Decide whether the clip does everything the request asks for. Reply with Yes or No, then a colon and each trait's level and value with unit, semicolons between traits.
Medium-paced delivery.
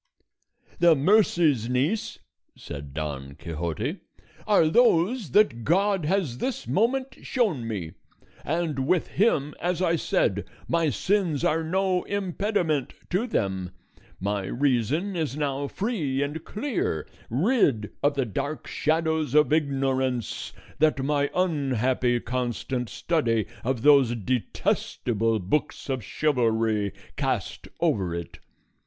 No: slow, 115 wpm